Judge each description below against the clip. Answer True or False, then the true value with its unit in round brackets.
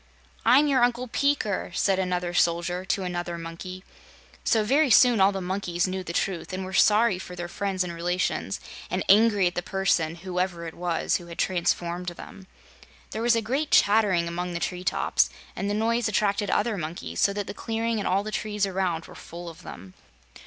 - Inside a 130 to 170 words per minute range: False (195 wpm)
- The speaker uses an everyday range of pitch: True (3.3 semitones)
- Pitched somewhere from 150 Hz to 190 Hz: True (185 Hz)